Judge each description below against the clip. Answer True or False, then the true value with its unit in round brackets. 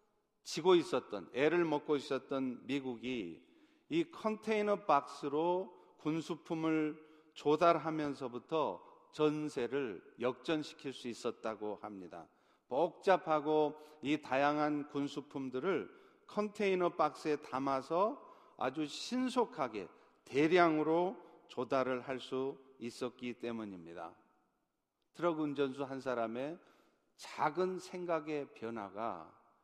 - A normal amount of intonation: True (4.9 semitones)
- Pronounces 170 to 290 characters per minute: True (225 characters per minute)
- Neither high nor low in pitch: True (150 Hz)